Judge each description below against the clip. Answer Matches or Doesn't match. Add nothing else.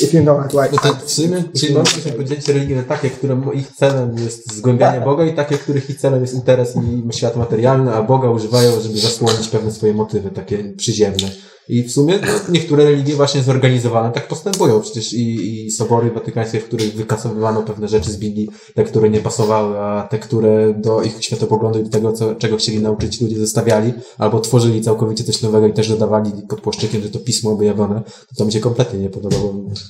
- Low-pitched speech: Matches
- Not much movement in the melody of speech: Doesn't match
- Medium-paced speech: Doesn't match